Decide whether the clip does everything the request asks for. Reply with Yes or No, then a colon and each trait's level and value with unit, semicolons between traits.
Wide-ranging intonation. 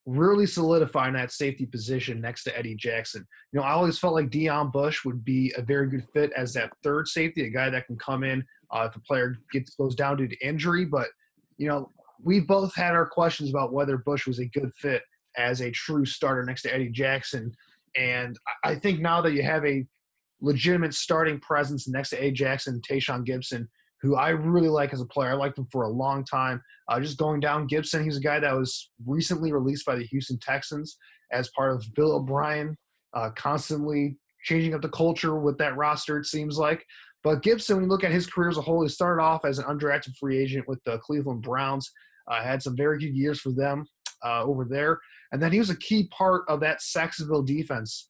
No: average, 3.0 semitones